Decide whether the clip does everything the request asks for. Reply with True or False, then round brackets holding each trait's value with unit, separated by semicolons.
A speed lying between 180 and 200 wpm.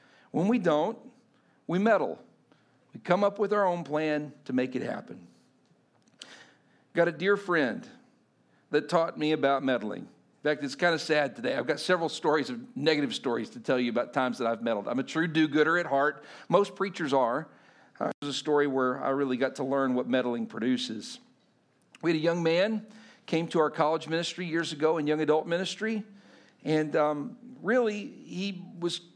True (185 wpm)